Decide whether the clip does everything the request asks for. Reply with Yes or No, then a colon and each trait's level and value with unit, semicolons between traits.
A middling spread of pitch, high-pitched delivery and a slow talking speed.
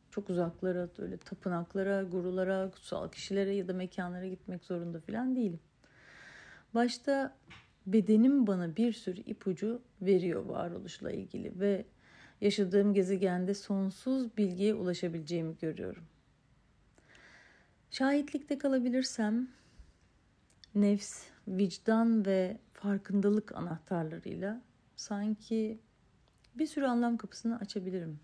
Yes: average, 3.3 semitones; high, 200 Hz; slow, 90 wpm